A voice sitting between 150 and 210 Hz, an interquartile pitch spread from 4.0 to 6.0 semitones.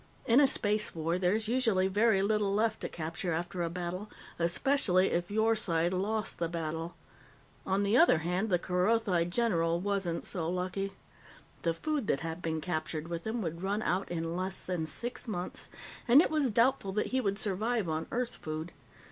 Yes: medium, 185 Hz; average, 4.4 semitones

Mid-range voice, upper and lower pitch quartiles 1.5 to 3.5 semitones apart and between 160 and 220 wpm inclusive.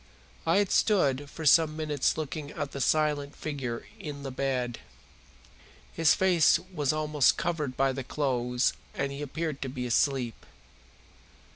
No: medium, 145 Hz; average, 2.7 semitones; average, 145 wpm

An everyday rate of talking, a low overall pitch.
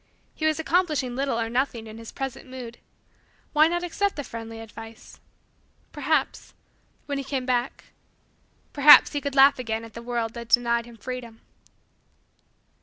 No: average, 155 wpm; very high, 250 Hz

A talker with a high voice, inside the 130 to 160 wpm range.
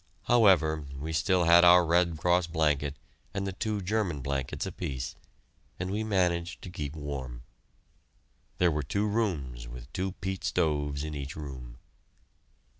No: very low, 80 Hz; average, 145 wpm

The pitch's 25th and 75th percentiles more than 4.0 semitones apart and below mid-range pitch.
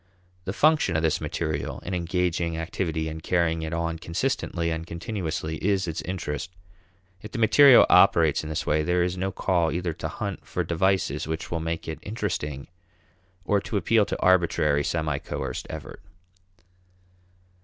No: average, 2.9 semitones; very low, 85 Hz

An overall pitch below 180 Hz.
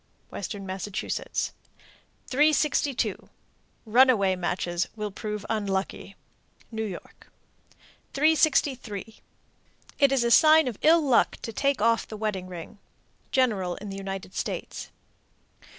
No: high, 215 Hz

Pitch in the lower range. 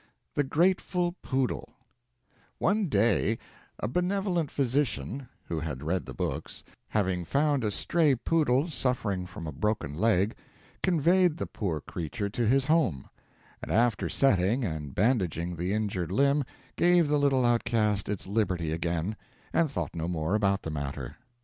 Yes: low, 110 Hz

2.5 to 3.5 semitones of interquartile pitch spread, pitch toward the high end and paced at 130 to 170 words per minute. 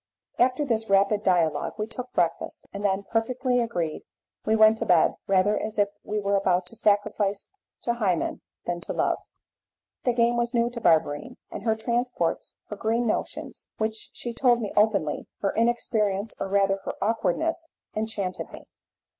Yes: average, 3.2 semitones; high, 215 Hz; average, 165 wpm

